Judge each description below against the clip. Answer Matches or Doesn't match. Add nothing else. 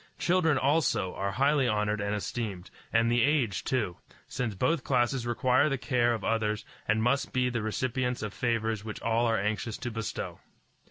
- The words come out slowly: Doesn't match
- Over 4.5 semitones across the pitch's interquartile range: Doesn't match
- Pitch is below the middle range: Matches